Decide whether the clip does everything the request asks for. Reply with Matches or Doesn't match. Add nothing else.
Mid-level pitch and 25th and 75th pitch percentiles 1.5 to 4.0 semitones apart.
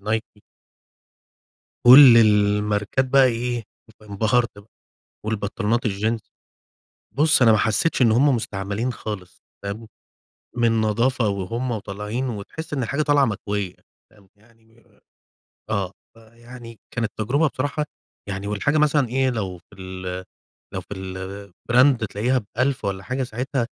Doesn't match